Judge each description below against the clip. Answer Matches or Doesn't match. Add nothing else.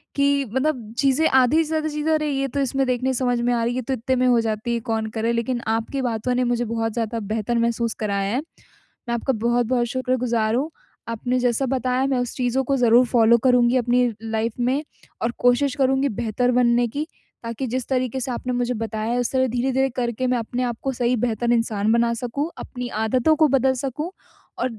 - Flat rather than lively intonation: Matches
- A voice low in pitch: Doesn't match